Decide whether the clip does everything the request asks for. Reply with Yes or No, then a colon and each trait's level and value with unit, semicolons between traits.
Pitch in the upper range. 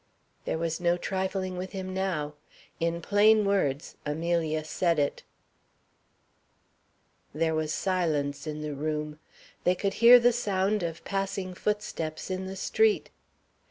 No: medium, 180 Hz